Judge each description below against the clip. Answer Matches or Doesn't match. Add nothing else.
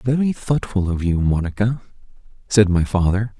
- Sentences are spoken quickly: Doesn't match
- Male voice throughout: Matches